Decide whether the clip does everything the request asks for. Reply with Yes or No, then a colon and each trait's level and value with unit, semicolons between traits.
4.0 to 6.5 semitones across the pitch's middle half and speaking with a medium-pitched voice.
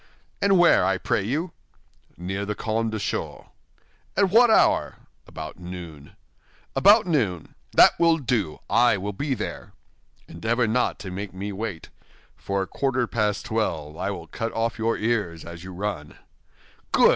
No: average, 4.9 semitones; low, 105 Hz